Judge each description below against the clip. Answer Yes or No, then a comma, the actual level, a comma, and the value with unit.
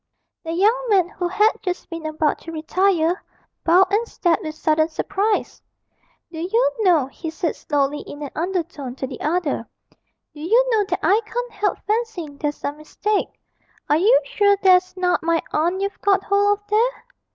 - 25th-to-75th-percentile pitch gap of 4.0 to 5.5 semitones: Yes, average, 4.6 semitones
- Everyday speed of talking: Yes, average, 175 wpm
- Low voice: No, very high, 360 Hz